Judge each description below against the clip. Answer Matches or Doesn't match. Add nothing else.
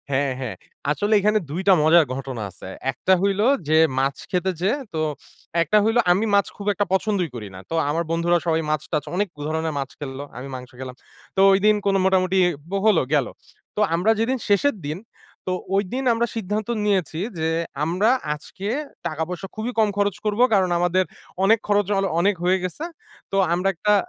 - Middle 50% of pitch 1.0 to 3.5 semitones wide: Doesn't match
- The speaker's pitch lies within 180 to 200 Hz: Matches